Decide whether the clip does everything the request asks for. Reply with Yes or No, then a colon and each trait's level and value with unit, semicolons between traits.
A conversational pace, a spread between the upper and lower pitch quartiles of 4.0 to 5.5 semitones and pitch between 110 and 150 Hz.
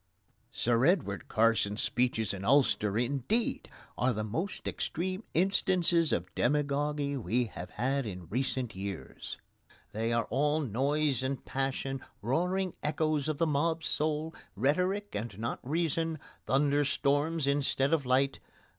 No: slow, 130 wpm; average, 4.9 semitones; medium, 140 Hz